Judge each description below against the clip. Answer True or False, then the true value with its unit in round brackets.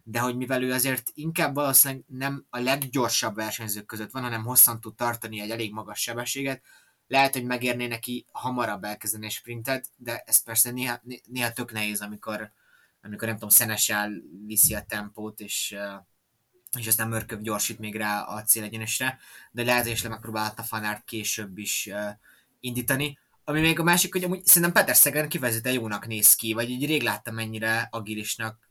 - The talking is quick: True (165 wpm)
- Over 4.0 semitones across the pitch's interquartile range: False (2.9 semitones)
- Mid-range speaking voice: False (115 Hz)